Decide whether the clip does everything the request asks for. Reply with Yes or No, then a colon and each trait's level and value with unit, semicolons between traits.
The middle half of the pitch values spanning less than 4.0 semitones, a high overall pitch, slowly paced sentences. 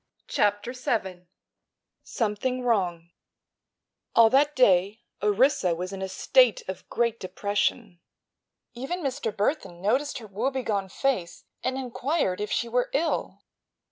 No: average, 5.3 semitones; high, 225 Hz; slow, 120 wpm